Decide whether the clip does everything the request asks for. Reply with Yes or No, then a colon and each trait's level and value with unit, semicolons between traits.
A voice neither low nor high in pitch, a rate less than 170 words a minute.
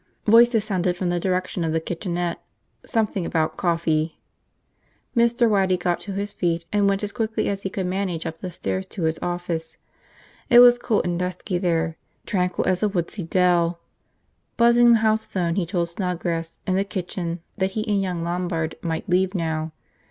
No: medium, 180 Hz; average, 180 wpm